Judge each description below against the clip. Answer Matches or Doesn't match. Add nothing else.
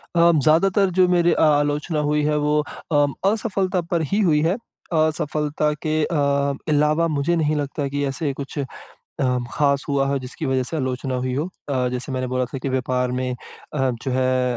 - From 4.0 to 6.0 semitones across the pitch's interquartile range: Doesn't match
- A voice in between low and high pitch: Matches